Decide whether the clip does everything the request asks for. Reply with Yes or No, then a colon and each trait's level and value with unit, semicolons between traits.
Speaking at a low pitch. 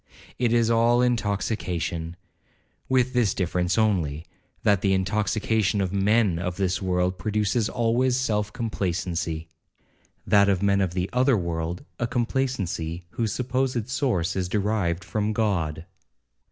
Yes: low, 100 Hz